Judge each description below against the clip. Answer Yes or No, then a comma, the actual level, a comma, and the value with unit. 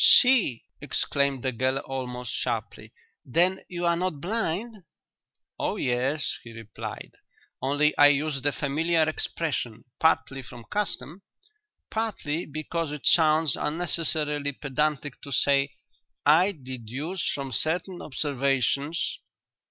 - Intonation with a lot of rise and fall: No, average, 3.8 semitones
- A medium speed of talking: No, slow, 115 wpm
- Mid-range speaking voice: Yes, medium, 145 Hz